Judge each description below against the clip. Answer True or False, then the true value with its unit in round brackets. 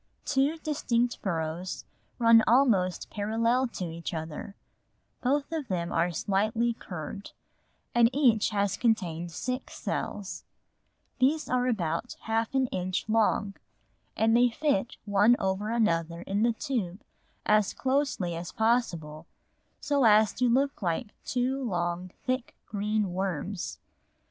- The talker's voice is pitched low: False (215 Hz)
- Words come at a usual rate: False (125 wpm)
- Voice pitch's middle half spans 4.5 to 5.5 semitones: True (5.2 semitones)